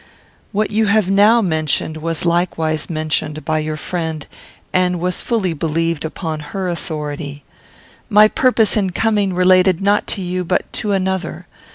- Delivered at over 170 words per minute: No, average, 150 wpm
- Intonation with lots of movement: No, average, 4.0 semitones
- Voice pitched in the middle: Yes, medium, 180 Hz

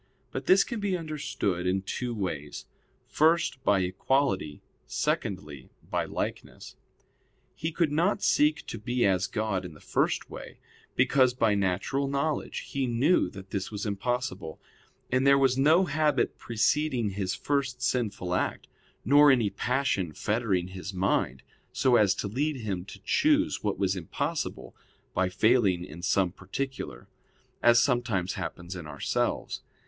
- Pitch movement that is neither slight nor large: No, wide, 6.6 semitones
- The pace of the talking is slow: No, average, 145 wpm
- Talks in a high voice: No, low, 110 Hz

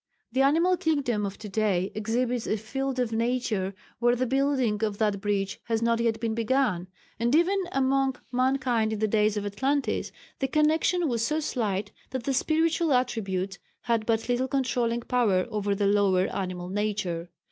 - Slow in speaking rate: No, average, 170 wpm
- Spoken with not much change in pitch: No, average, 4.3 semitones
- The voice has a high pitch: Yes, high, 230 Hz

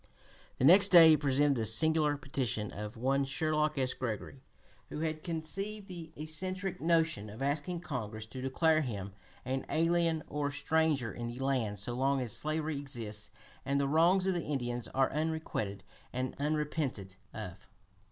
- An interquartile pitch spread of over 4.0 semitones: Yes, average, 4.6 semitones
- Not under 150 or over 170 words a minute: Yes, average, 160 wpm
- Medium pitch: Yes, medium, 145 Hz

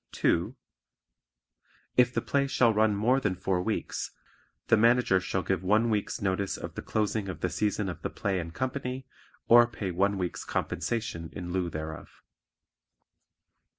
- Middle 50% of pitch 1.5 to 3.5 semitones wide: No, average, 4.1 semitones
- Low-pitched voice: Yes, low, 100 Hz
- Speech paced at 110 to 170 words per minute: Yes, average, 155 wpm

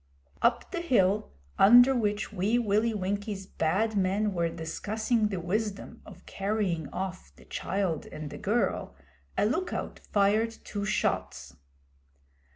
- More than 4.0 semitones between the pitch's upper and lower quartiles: No, average, 2.7 semitones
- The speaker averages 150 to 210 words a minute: No, slow, 135 wpm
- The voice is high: Yes, high, 205 Hz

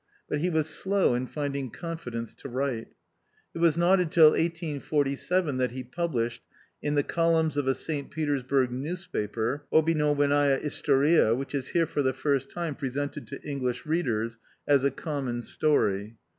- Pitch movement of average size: Yes, average, 3.7 semitones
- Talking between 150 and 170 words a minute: Yes, average, 155 wpm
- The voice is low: No, medium, 145 Hz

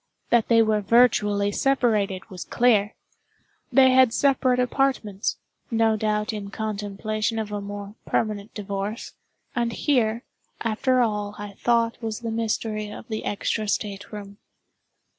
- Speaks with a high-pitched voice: Yes, high, 215 Hz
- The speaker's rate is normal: No, slow, 130 wpm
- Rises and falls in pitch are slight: Yes, narrow, 2.3 semitones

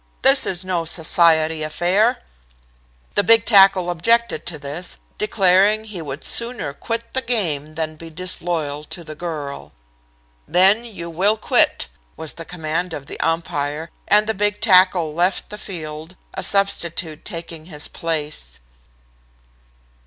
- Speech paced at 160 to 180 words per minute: No, average, 140 wpm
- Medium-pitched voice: Yes, medium, 175 Hz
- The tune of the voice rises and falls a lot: No, average, 4.2 semitones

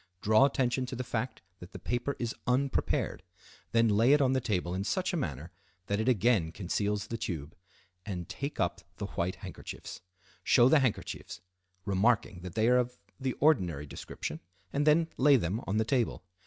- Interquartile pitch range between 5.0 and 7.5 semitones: Yes, wide, 5.5 semitones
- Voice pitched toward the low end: Yes, low, 115 Hz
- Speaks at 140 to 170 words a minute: No, average, 180 wpm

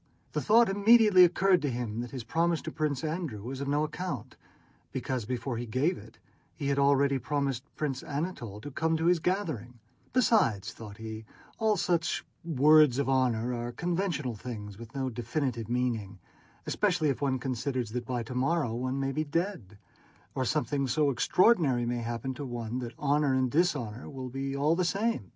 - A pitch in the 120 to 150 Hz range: Yes, low, 135 Hz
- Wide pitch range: No, average, 5.0 semitones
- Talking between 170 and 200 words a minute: Yes, average, 175 wpm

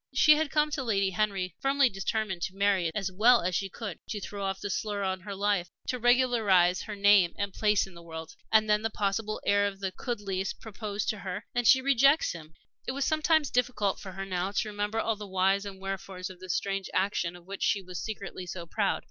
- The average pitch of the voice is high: Yes, high, 200 Hz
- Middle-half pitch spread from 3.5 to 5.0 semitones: No, average, 2.8 semitones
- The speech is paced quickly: Yes, fast, 235 wpm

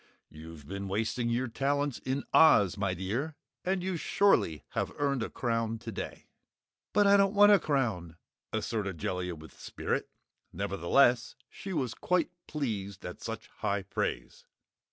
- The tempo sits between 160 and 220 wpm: No, average, 145 wpm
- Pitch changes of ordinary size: No, wide, 6.7 semitones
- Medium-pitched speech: No, low, 115 Hz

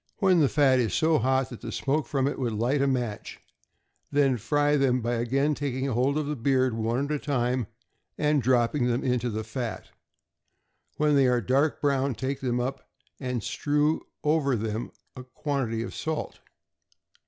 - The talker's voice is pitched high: No, low, 130 Hz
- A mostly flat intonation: No, average, 3.1 semitones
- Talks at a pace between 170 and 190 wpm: Yes, average, 175 wpm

